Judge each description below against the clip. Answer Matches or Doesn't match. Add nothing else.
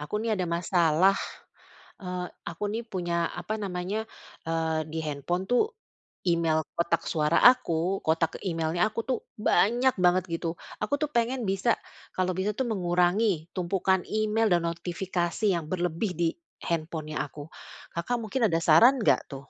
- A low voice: Doesn't match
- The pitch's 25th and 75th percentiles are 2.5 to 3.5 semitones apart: Doesn't match